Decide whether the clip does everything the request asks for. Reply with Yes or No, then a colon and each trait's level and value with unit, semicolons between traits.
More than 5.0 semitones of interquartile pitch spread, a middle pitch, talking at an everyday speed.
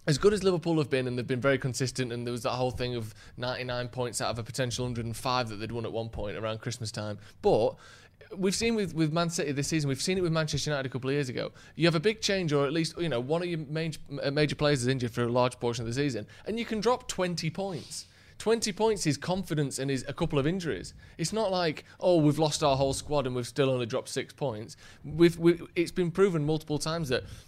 No: wide, 5.4 semitones; medium, 145 Hz; fast, 260 wpm